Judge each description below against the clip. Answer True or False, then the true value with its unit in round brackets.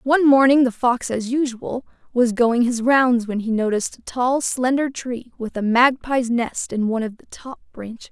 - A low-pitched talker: False (245 Hz)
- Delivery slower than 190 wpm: False (200 wpm)